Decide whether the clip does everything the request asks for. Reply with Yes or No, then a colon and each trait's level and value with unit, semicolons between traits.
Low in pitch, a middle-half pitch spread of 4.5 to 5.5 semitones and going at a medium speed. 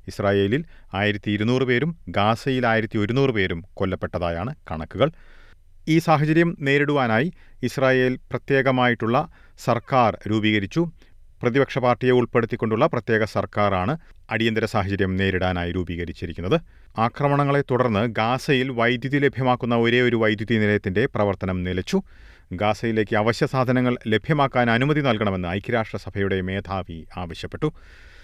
Yes: low, 115 Hz; average, 4.8 semitones; average, 100 wpm